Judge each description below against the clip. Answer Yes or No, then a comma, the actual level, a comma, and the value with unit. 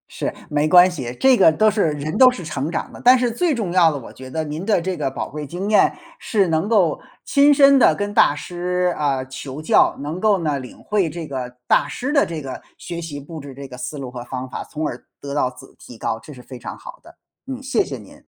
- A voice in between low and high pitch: Yes, medium, 160 Hz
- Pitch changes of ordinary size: No, wide, 6.6 semitones